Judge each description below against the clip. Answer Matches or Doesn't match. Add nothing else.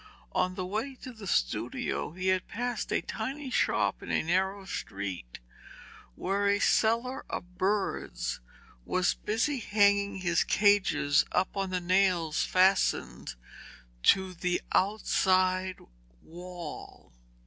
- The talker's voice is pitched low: Doesn't match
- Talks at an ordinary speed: Doesn't match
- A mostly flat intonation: Matches